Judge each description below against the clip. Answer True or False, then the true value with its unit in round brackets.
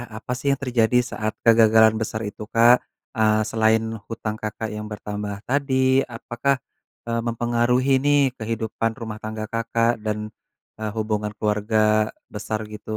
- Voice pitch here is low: True (110 Hz)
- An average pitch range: False (1.5 semitones)